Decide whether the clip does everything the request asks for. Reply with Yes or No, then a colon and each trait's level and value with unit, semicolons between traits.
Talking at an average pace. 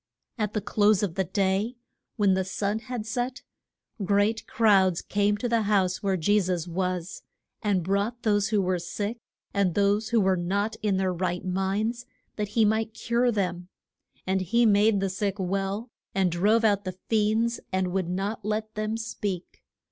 Yes: average, 175 wpm